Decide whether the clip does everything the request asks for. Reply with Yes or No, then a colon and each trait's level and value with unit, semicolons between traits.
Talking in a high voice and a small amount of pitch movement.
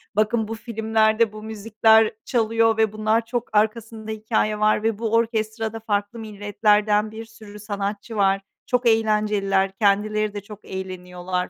Yes: high, 215 Hz; narrow, 1.4 semitones